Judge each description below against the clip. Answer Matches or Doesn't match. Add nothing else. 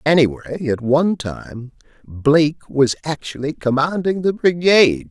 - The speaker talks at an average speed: Doesn't match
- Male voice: Matches